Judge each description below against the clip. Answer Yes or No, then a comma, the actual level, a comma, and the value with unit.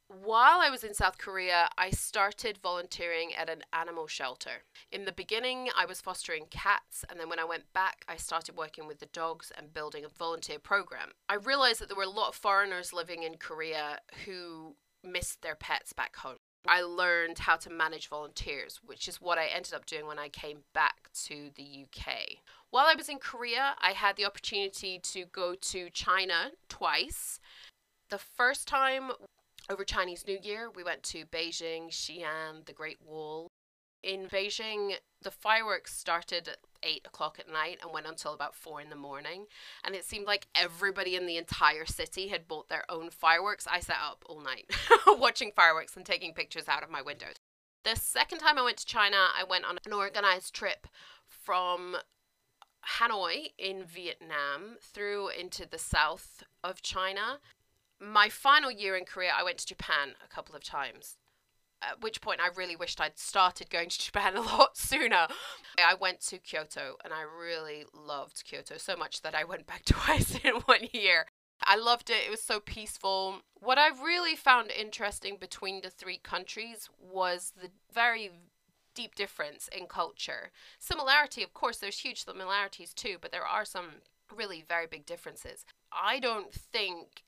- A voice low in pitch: No, medium, 185 Hz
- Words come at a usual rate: Yes, average, 180 wpm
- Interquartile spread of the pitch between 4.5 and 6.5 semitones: No, average, 4.0 semitones